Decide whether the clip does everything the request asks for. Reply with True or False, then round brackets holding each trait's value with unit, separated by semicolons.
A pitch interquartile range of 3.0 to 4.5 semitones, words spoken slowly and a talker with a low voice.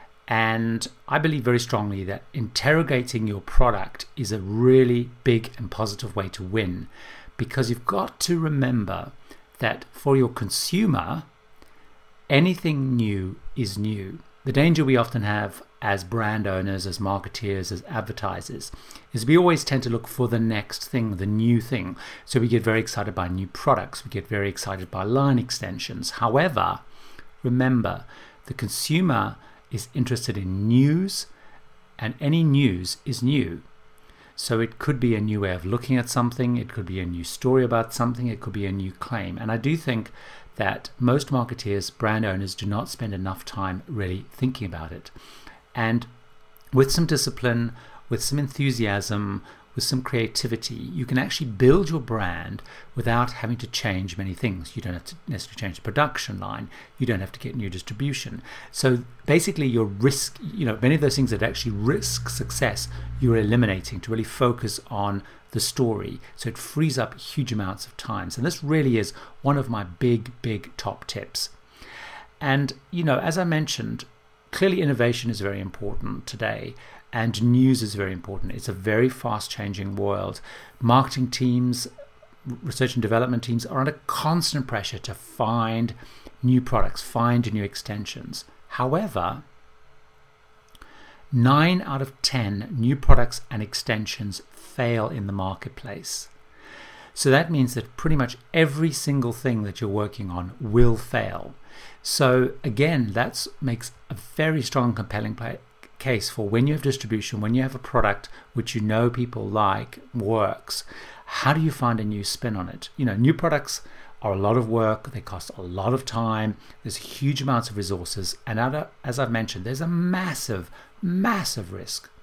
False (3.9 semitones; 165 wpm; 120 Hz)